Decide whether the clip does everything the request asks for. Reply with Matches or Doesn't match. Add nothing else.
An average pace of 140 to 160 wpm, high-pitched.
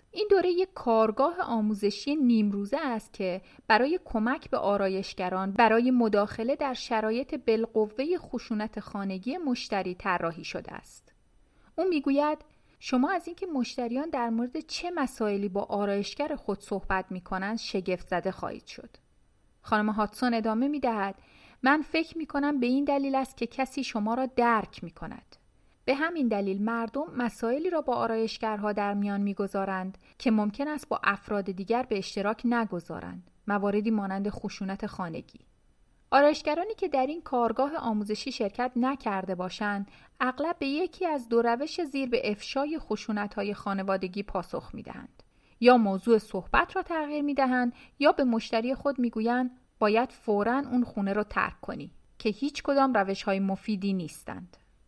Matches